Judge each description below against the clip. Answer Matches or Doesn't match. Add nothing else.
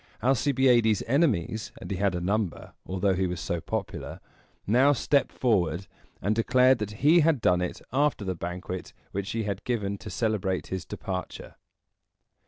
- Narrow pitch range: Doesn't match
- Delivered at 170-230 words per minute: Doesn't match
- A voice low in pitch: Matches